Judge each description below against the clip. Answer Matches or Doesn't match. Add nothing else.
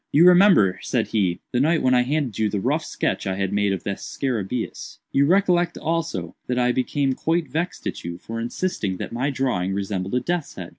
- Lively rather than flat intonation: Matches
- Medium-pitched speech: Doesn't match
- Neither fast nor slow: Doesn't match